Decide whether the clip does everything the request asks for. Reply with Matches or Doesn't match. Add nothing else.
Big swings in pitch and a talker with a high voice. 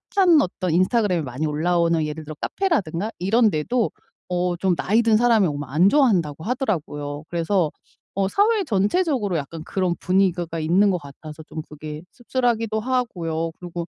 Doesn't match